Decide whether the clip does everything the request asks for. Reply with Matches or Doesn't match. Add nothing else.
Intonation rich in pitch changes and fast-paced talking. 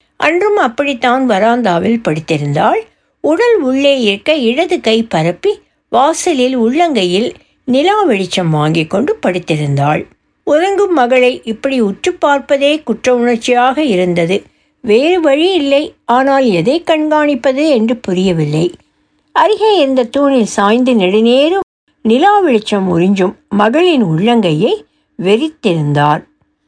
Doesn't match